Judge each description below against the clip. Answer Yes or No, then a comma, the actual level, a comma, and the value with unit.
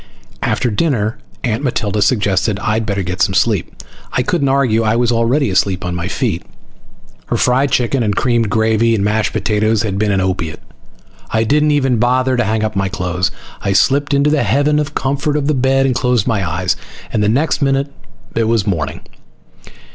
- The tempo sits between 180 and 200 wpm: Yes, average, 190 wpm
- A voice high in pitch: No, low, 115 Hz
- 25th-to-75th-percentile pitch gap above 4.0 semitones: Yes, average, 4.9 semitones